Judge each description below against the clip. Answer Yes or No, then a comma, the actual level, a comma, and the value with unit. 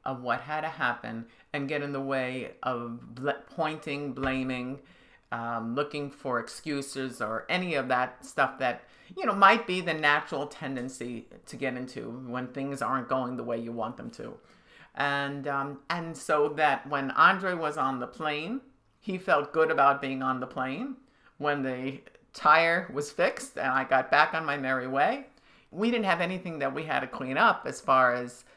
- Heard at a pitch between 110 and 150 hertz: Yes, medium, 140 Hz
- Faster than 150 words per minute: Yes, average, 185 wpm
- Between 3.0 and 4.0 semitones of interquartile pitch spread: Yes, average, 3.6 semitones